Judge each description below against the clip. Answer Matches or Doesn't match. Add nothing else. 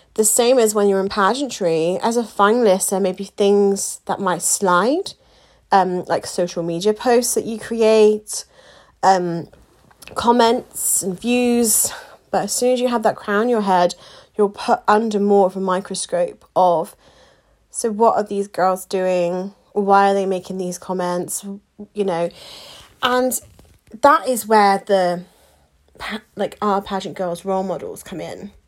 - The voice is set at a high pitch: Matches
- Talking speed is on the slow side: Doesn't match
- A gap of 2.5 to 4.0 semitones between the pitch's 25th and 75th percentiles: Matches